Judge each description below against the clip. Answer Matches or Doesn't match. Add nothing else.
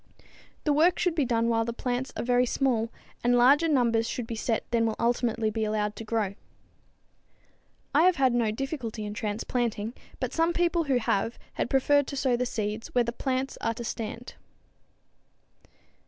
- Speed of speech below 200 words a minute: Matches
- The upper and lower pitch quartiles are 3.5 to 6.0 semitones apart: Doesn't match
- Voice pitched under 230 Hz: Doesn't match